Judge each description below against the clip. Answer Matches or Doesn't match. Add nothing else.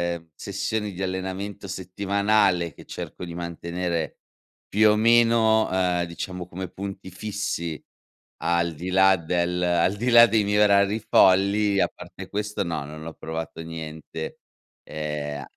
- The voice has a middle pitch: Doesn't match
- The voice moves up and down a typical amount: Matches